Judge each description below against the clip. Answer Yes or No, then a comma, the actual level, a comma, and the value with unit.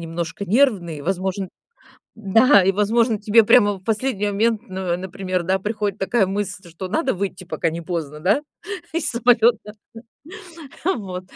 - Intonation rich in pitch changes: No, average, 3.3 semitones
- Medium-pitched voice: No, high, 195 Hz